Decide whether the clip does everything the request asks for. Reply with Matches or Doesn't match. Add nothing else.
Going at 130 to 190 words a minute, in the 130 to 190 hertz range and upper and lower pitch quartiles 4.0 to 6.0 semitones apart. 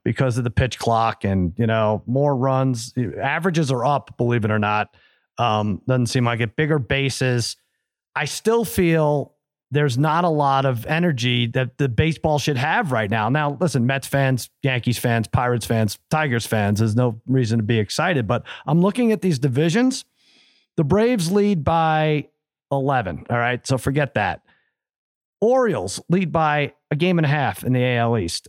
Matches